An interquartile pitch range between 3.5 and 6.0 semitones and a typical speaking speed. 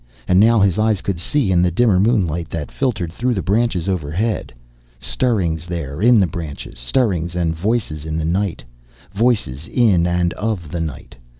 Yes: average, 4.9 semitones; average, 175 wpm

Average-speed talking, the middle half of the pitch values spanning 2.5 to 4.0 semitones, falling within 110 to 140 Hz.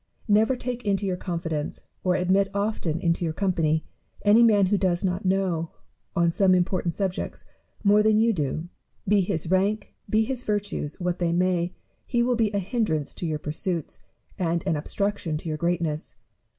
No: average, 175 wpm; average, 3.6 semitones; medium, 185 Hz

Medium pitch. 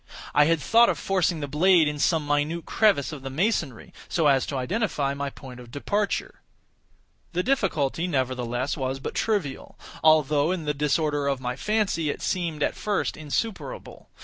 Yes: medium, 150 Hz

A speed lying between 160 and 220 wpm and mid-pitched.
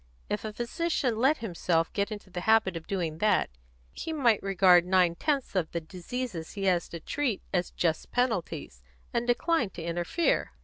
No: average, 175 wpm; high, 195 Hz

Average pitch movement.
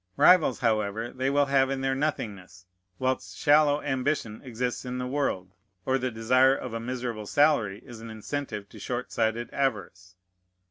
Yes: average, 3.5 semitones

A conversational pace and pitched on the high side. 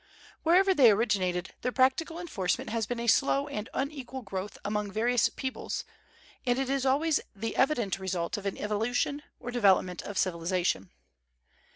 Yes: average, 155 wpm; high, 230 Hz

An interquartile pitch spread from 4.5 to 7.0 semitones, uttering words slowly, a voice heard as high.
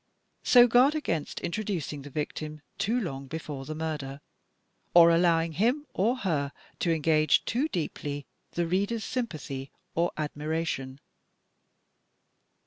No: wide, 5.6 semitones; slow, 120 wpm; medium, 165 Hz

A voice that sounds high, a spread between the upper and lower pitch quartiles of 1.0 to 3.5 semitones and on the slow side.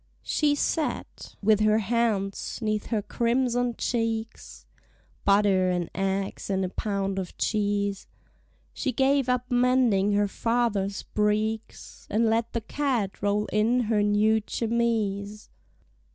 Yes: high, 215 Hz; narrow, 2.6 semitones; slow, 125 wpm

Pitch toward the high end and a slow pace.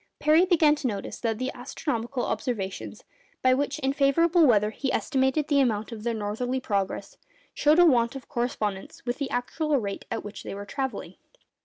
No: very high, 255 Hz; average, 180 wpm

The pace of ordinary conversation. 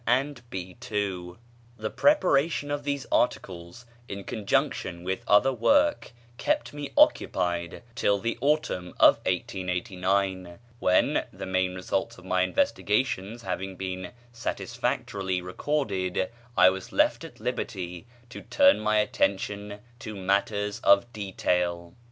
No: slow, 120 wpm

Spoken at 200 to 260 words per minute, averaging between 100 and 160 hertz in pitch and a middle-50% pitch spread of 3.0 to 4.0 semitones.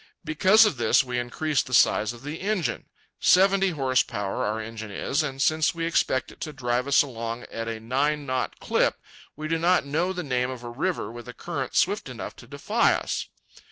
No: fast, 205 wpm; low, 135 Hz; average, 5.0 semitones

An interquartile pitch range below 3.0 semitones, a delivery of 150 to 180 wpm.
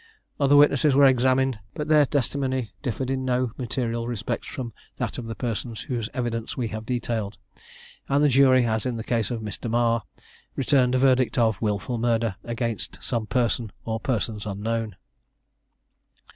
Yes: narrow, 2.6 semitones; average, 160 wpm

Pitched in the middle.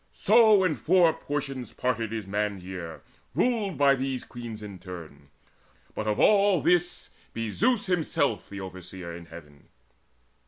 No: low, 115 Hz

